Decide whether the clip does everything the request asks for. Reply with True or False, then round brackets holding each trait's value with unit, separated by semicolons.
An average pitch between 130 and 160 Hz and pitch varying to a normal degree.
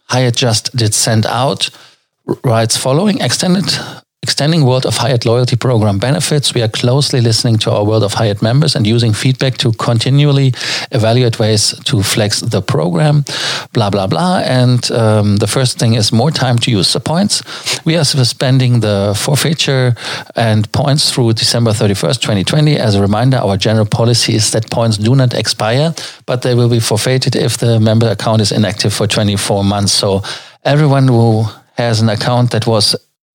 False (120 Hz; 3.3 semitones)